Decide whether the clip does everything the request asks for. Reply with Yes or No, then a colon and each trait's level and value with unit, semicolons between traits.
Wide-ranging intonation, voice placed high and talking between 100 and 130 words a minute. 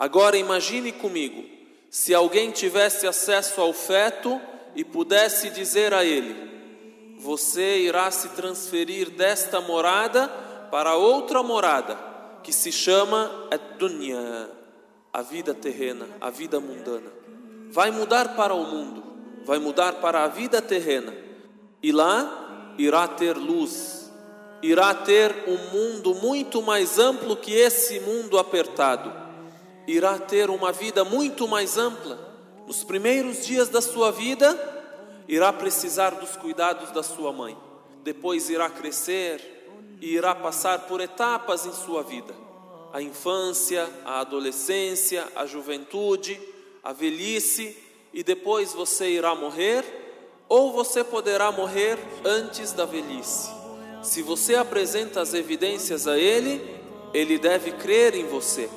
Yes: wide, 5.8 semitones; high, 200 Hz; average, 125 wpm